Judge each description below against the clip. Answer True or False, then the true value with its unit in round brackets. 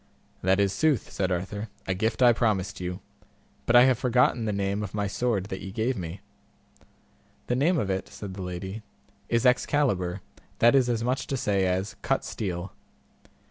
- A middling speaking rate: True (180 wpm)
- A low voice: True (105 Hz)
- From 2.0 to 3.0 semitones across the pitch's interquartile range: False (4.4 semitones)